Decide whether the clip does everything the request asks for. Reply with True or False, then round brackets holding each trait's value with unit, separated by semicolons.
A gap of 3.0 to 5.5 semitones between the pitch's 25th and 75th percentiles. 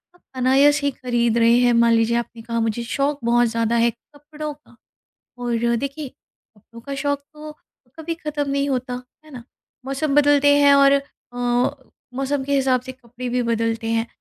True (3.4 semitones)